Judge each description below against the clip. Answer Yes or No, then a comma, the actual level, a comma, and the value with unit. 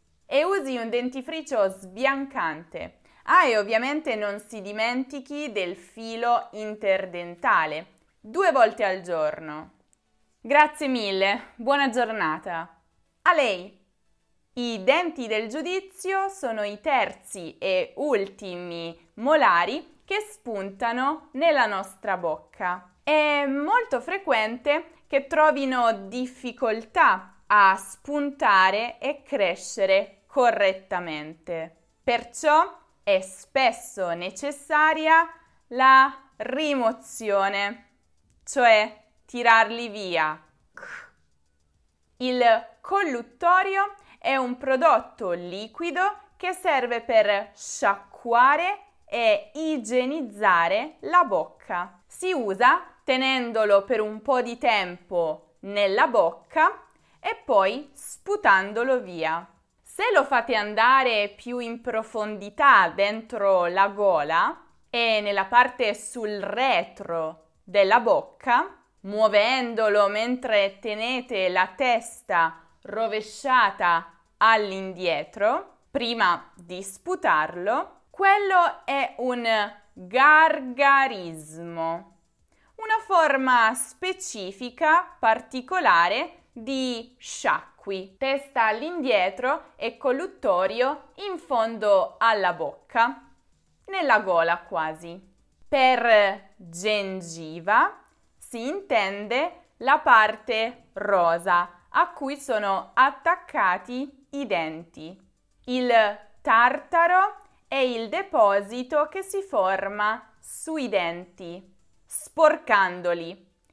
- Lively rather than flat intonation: Yes, wide, 6.8 semitones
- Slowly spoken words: Yes, slow, 85 wpm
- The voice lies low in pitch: No, high, 230 Hz